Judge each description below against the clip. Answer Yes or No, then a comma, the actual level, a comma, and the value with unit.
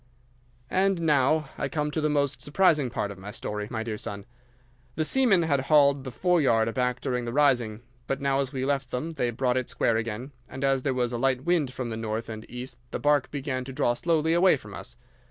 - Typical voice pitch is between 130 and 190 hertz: Yes, low, 135 Hz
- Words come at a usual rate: No, fast, 225 wpm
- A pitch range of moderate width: Yes, average, 3.8 semitones